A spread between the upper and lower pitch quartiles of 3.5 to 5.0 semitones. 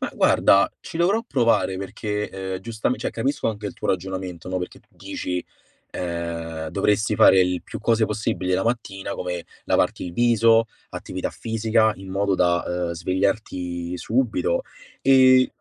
Yes: average, 4.0 semitones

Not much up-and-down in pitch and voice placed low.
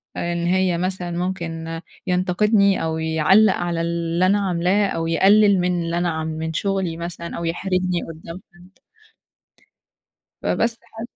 No: narrow, 2.3 semitones; medium, 175 Hz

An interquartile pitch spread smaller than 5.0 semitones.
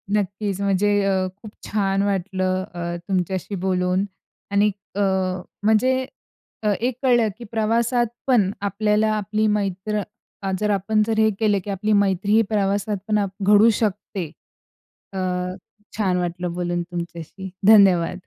Yes: narrow, 2.4 semitones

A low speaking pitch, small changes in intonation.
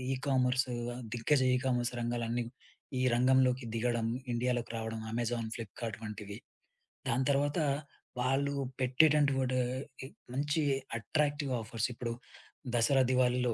Yes: low, 125 Hz; narrow, 2.3 semitones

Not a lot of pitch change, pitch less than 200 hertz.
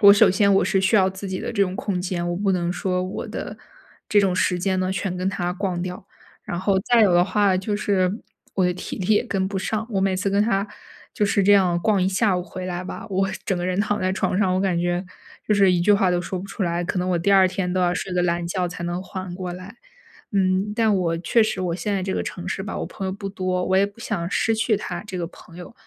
Yes: narrow, 1.9 semitones; high, 190 Hz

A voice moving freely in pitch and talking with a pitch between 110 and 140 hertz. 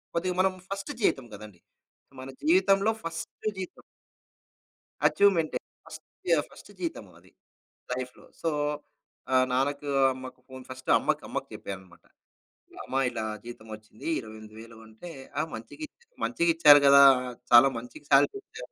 Yes: wide, 6.7 semitones; low, 135 Hz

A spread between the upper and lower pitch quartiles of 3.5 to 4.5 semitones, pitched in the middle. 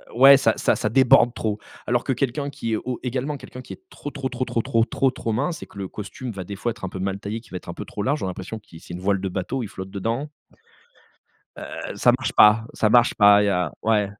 No: average, 4.2 semitones; low, 115 Hz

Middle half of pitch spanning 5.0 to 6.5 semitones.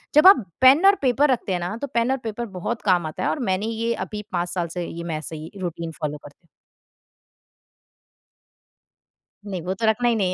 Yes: wide, 5.5 semitones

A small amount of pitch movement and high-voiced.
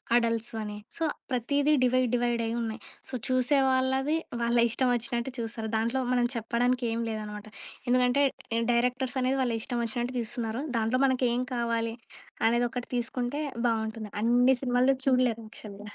Yes: narrow, 1.8 semitones; high, 240 Hz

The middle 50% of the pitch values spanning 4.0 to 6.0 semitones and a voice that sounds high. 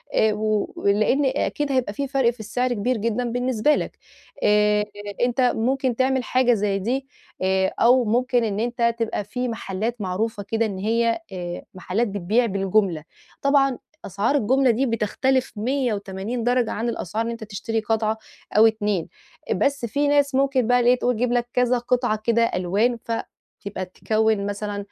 No: average, 3.2 semitones; high, 230 Hz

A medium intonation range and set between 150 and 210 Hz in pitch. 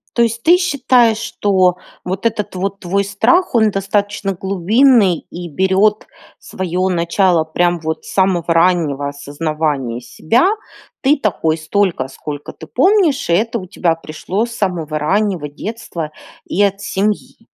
Yes: average, 4.5 semitones; high, 190 Hz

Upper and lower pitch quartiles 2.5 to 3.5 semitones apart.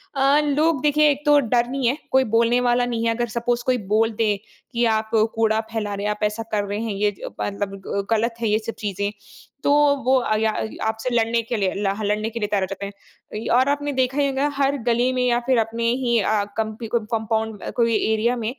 Yes: average, 2.8 semitones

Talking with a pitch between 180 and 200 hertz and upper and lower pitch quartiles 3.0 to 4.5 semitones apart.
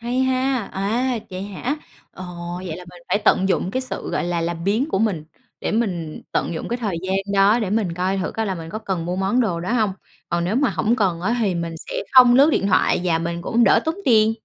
No: high, 195 Hz; average, 5.0 semitones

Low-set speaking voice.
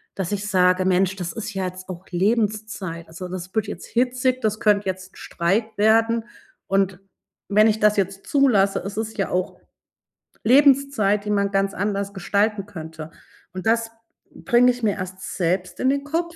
No: high, 200 Hz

